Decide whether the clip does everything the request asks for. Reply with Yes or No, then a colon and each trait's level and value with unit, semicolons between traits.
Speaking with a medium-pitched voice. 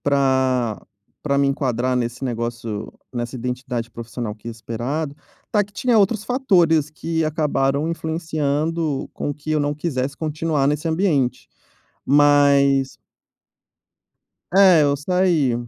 Yes: medium, 145 Hz